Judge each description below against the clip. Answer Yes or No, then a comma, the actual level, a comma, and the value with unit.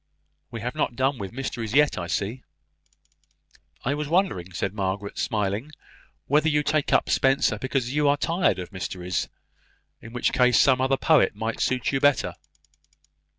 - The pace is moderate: Yes, average, 165 wpm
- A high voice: No, low, 125 Hz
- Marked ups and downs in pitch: Yes, wide, 5.8 semitones